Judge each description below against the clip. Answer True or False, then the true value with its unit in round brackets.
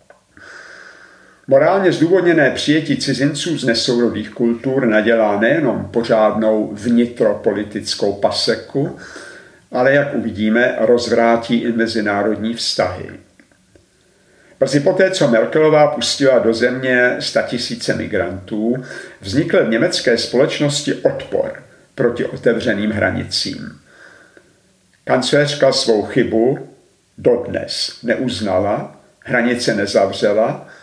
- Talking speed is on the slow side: True (85 wpm)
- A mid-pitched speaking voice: False (120 Hz)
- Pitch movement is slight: False (4.3 semitones)